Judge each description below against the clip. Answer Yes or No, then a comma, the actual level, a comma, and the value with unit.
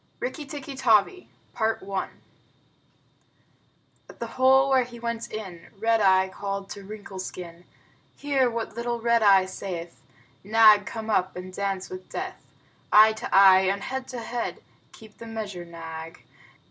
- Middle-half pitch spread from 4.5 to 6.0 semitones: No, average, 3.7 semitones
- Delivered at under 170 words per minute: Yes, average, 145 wpm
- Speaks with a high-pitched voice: Yes, high, 215 Hz